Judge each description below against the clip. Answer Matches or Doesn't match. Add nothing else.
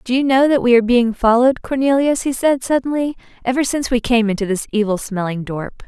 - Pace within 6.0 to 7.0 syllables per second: Matches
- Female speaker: Matches